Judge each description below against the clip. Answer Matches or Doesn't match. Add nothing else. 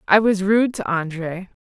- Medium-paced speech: Matches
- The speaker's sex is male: Doesn't match